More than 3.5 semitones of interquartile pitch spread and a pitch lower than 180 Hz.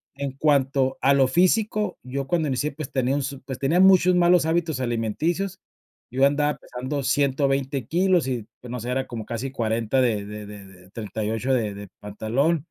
Yes: average, 4.5 semitones; low, 135 Hz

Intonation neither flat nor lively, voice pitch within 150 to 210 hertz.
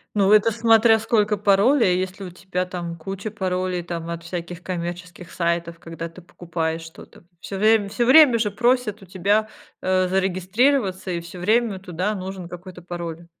Yes: average, 3.3 semitones; medium, 185 Hz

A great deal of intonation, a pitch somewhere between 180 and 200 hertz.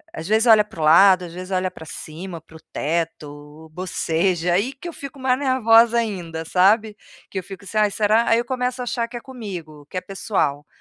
Yes: wide, 5.8 semitones; high, 195 Hz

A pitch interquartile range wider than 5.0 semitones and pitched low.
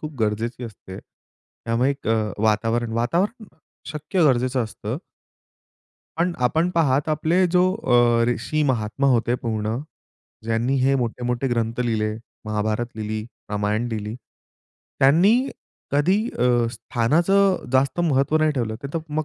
Yes: wide, 5.4 semitones; low, 125 Hz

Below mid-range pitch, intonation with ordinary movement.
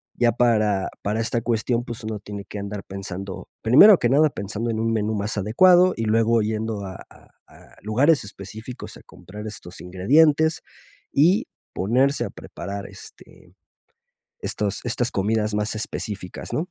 Yes: low, 110 Hz; average, 3.2 semitones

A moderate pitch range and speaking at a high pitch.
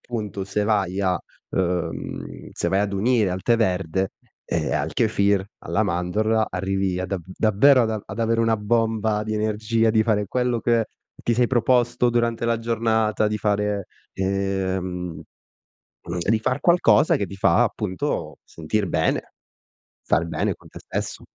No: average, 3.0 semitones; low, 105 Hz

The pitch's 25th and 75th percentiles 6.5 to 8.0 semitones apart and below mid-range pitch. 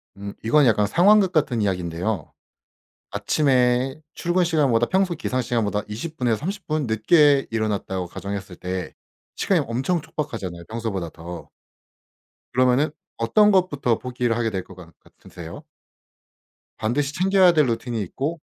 Yes: wide, 6.9 semitones; low, 120 Hz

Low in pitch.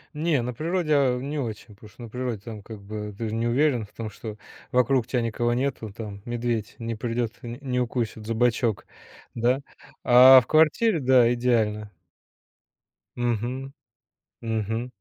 Yes: low, 120 Hz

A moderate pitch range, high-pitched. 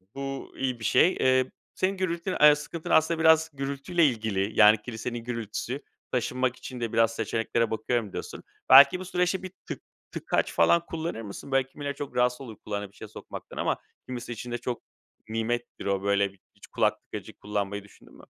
No: average, 4.7 semitones; low, 125 Hz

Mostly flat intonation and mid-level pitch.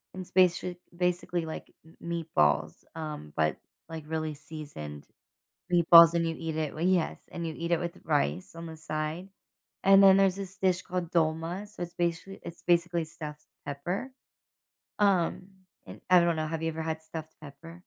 Yes: narrow, 2.2 semitones; medium, 165 Hz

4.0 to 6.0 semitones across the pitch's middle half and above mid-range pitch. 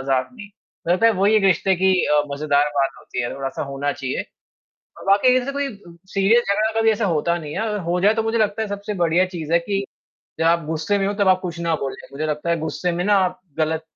No: average, 4.8 semitones; medium, 180 Hz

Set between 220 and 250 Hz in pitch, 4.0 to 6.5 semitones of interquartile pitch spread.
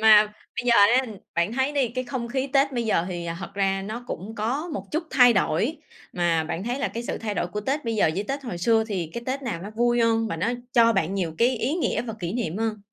Yes: high, 225 Hz; average, 4.3 semitones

